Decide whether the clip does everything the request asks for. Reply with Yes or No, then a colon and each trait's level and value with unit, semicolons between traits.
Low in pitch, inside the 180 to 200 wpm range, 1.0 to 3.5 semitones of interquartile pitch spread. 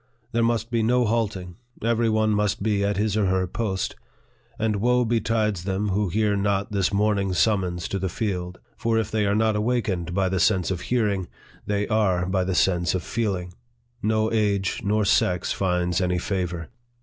Yes: low, 100 Hz; average, 185 wpm; average, 2.9 semitones